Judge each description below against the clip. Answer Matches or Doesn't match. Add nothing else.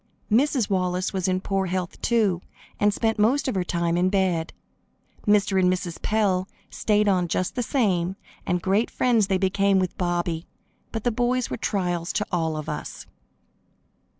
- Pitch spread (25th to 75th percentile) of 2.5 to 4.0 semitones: Matches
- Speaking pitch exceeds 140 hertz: Matches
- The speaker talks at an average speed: Matches